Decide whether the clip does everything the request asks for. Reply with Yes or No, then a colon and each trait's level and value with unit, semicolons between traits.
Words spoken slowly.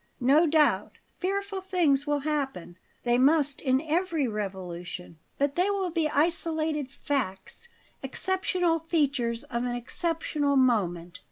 Yes: slow, 120 wpm